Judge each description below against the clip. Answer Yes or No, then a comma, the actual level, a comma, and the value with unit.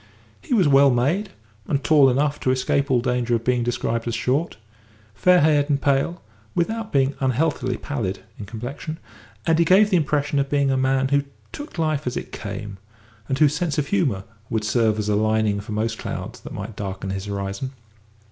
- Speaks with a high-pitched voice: No, low, 135 Hz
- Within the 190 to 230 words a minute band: Yes, average, 195 wpm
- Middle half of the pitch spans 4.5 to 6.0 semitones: Yes, average, 4.8 semitones